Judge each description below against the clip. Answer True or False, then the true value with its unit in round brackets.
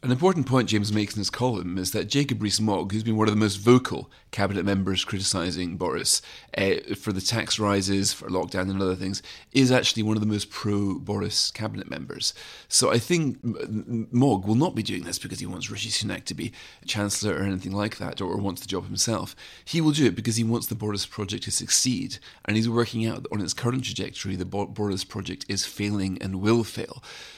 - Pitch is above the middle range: False (105 Hz)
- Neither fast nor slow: False (220 wpm)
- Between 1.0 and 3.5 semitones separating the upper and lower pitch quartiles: True (3.0 semitones)